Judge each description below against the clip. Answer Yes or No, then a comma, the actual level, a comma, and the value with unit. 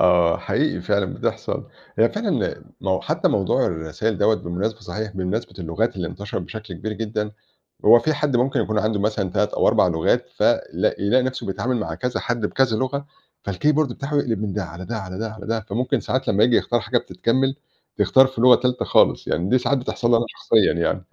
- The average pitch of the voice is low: Yes, low, 110 Hz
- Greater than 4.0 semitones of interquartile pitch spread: Yes, average, 4.4 semitones